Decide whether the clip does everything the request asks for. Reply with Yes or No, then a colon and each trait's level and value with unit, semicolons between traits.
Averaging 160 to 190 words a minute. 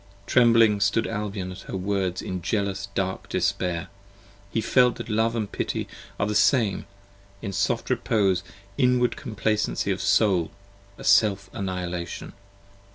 No: average, 140 wpm